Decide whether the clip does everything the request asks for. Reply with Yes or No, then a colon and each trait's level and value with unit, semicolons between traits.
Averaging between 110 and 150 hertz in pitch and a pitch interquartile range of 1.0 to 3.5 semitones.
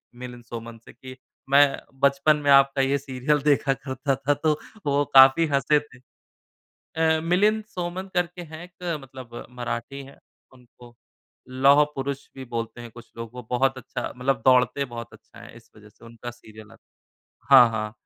Yes: low, 135 Hz; average, 2.9 semitones